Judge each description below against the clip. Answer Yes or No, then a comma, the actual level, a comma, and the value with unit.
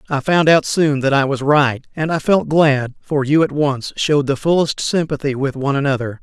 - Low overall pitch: No, medium, 145 Hz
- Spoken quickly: Yes, fast, 220 wpm